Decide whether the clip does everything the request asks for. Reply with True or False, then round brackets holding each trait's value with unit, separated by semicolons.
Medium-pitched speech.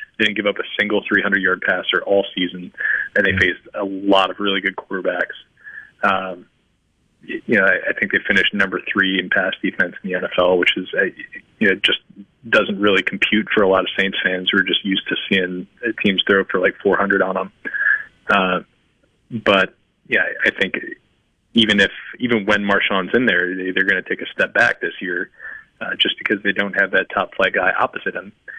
False (95 Hz)